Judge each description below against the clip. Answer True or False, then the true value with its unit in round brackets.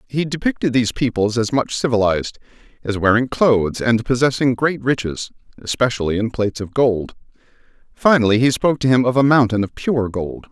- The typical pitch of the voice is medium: False (120 Hz)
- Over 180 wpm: False (170 wpm)